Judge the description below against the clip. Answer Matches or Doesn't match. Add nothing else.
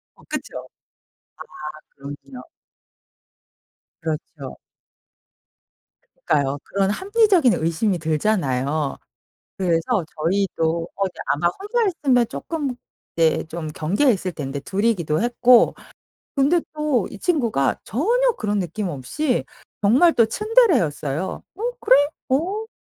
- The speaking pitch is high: Matches